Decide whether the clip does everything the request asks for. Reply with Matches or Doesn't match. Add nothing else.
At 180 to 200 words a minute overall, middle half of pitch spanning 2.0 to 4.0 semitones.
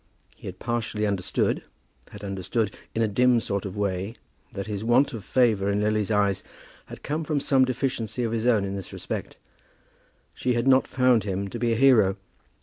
Matches